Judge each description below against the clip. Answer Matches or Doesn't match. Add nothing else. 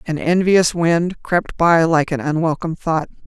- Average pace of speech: Matches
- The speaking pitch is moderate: Matches